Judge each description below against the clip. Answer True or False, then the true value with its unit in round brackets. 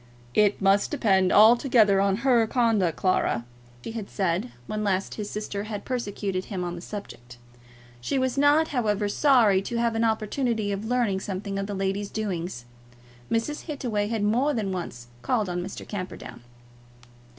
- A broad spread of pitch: False (3.3 semitones)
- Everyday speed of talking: True (160 wpm)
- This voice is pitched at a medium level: False (205 Hz)